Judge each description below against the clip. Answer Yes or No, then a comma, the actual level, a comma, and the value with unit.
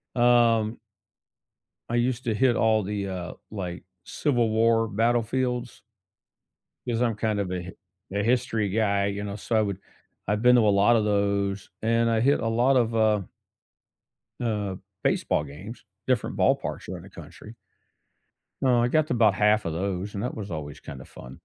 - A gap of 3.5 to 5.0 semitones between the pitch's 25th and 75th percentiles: No, average, 2.9 semitones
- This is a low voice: Yes, low, 110 Hz